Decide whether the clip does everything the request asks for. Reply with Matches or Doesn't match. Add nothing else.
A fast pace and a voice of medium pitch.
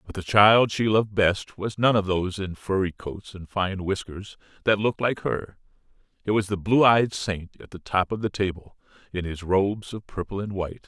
Doesn't match